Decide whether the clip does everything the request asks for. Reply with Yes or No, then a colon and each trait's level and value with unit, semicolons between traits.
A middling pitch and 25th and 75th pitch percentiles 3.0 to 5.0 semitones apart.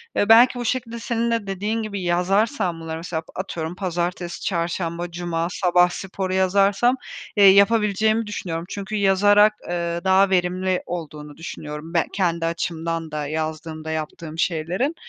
Yes: medium, 180 Hz; average, 3.5 semitones